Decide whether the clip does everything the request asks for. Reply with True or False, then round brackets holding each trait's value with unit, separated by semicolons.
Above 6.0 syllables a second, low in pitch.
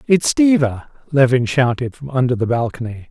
False (5.4 syllables/s; 130 Hz)